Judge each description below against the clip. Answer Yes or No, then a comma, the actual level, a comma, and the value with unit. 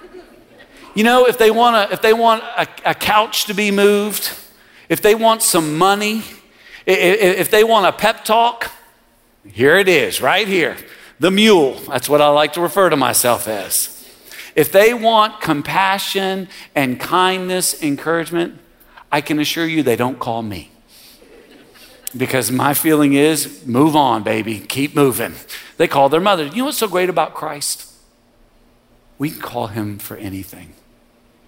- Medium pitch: Yes, medium, 165 Hz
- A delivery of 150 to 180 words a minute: Yes, average, 160 wpm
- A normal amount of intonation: No, wide, 8.0 semitones